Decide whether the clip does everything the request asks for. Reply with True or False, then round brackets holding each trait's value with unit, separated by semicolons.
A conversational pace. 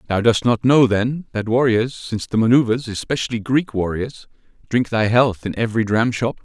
True (175 wpm)